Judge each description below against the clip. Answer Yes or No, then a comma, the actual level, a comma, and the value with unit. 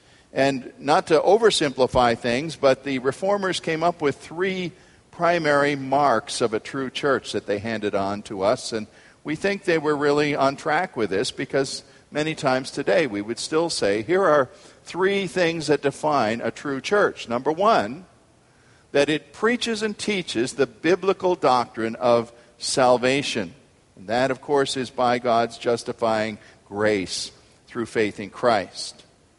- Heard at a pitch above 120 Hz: Yes, medium, 140 Hz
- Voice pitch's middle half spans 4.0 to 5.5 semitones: Yes, average, 5.2 semitones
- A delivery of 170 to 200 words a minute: No, average, 155 wpm